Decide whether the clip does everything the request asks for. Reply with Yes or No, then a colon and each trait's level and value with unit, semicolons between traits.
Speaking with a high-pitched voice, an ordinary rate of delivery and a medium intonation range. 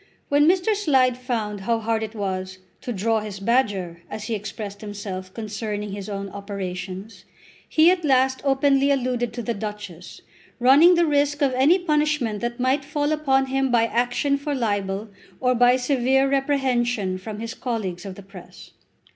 Yes: high, 240 Hz; average, 165 wpm; average, 4.9 semitones